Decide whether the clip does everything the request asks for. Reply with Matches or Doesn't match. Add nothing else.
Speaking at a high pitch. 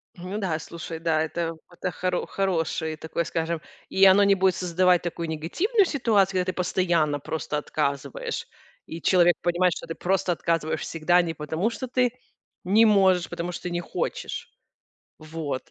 Doesn't match